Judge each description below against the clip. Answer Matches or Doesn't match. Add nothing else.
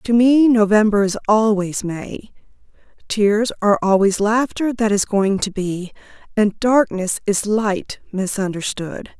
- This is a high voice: Matches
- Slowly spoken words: Matches